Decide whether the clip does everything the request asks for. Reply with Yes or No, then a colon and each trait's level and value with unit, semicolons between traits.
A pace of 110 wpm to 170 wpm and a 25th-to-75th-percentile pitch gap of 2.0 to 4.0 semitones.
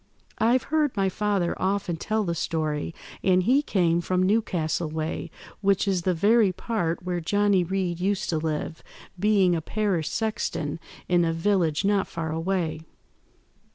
Yes: average, 155 wpm; average, 3.7 semitones